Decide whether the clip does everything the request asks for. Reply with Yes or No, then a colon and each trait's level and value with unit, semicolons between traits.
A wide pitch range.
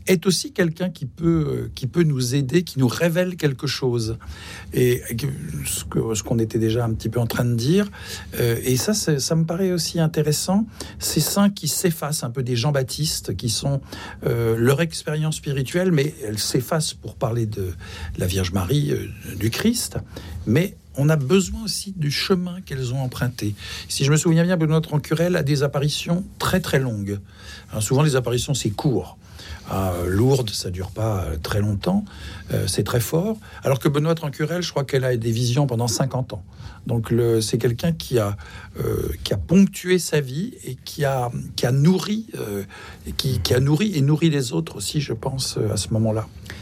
Yes: wide, 6.4 semitones